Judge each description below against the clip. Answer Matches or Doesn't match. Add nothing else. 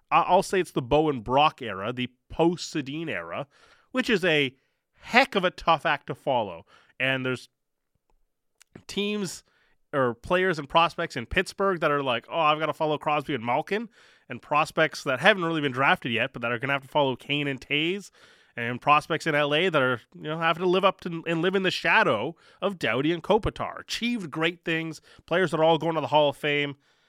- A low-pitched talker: Doesn't match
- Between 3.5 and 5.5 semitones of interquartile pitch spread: Matches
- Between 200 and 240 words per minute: Matches